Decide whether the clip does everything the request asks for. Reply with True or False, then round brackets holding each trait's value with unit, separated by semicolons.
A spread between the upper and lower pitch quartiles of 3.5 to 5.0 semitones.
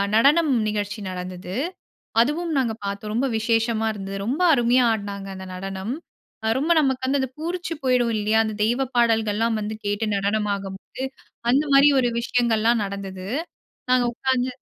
True (4.0 semitones)